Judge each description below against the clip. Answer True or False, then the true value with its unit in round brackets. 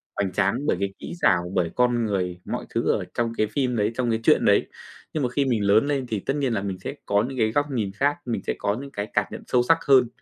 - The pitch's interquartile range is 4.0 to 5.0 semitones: True (4.5 semitones)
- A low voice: True (115 Hz)